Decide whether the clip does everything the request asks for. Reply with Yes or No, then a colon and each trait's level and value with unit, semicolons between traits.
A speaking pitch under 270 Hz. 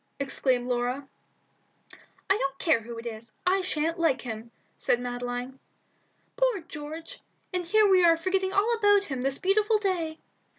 No: very high, 320 Hz